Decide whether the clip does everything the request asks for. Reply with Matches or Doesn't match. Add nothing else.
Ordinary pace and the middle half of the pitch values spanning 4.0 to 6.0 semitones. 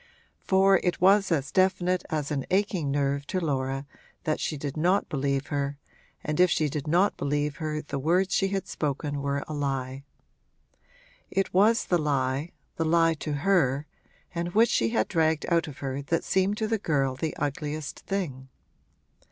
Matches